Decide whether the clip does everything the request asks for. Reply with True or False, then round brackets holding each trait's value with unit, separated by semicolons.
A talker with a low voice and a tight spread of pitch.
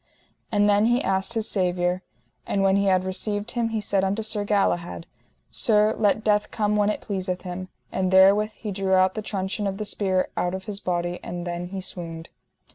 False (195 Hz; 2.1 semitones)